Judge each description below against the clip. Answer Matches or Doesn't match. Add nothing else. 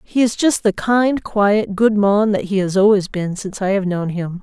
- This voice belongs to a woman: Matches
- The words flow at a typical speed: Doesn't match